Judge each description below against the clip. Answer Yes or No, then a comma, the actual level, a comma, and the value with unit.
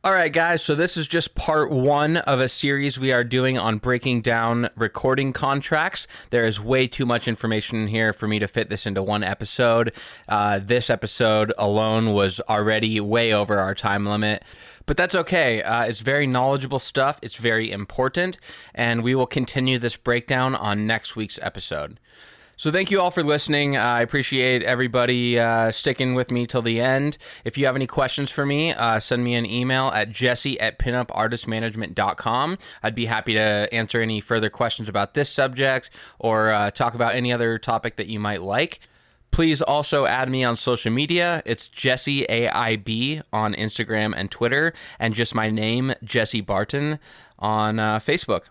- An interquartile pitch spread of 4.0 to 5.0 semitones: No, average, 3.3 semitones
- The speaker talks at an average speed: Yes, average, 180 wpm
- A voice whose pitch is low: Yes, low, 120 Hz